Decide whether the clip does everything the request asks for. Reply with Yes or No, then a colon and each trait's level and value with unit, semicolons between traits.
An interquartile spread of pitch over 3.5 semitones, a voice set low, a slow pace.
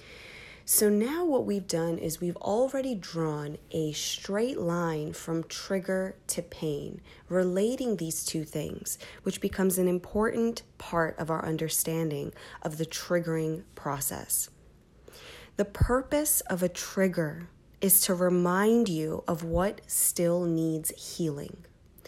No: average, 3.9 semitones; medium, 175 Hz; slow, 125 wpm